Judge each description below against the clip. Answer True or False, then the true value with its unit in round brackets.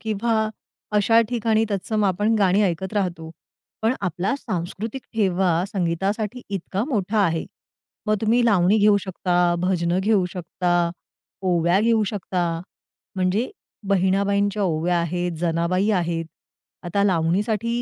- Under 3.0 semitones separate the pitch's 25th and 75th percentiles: False (3.3 semitones)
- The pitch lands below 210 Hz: True (190 Hz)